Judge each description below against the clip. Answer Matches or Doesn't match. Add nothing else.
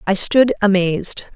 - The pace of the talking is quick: Doesn't match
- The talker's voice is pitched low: Doesn't match